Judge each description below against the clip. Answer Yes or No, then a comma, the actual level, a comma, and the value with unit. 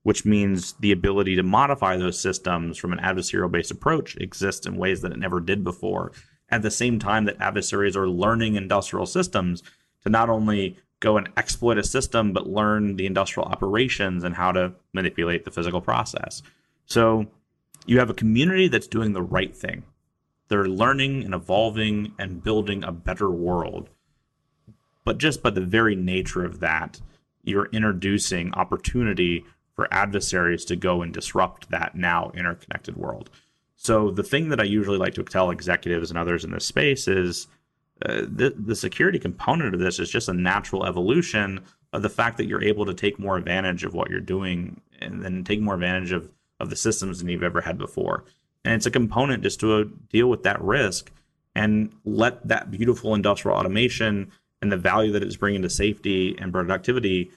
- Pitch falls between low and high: No, low, 100 Hz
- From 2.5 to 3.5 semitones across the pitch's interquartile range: Yes, average, 3.2 semitones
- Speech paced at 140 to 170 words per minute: No, average, 180 wpm